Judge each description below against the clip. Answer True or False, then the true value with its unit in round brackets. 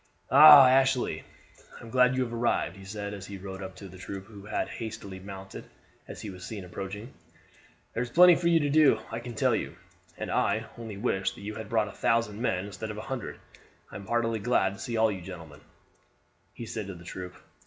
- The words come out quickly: True (225 wpm)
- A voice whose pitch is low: True (105 Hz)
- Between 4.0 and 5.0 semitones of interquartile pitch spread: False (3.6 semitones)